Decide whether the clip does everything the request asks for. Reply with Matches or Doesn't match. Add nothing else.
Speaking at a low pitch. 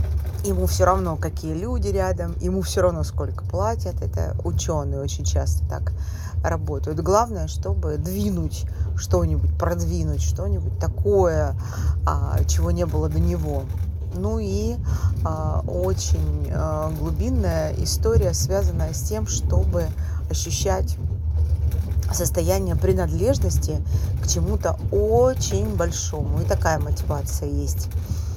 Matches